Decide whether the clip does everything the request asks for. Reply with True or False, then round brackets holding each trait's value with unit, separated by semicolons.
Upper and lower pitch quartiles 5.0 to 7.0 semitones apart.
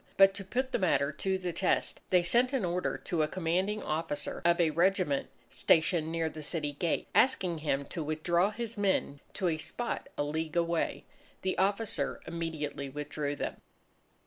False (3.8 semitones)